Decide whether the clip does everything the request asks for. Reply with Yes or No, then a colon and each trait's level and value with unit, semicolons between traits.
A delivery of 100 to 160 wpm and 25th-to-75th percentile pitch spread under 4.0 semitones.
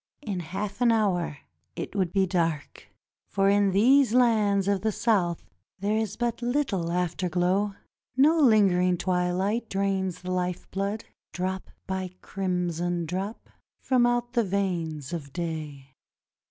Yes: slow, 135 wpm; average, 3.2 semitones